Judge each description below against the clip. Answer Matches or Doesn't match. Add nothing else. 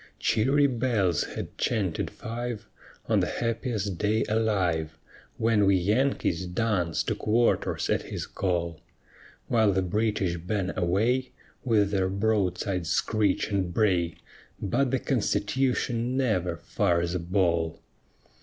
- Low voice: Matches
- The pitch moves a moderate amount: Matches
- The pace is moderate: Doesn't match